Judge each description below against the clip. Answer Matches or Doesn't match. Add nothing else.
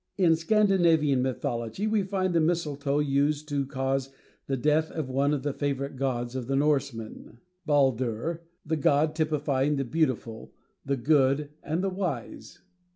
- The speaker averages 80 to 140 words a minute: Doesn't match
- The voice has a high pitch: Doesn't match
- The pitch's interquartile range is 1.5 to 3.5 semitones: Matches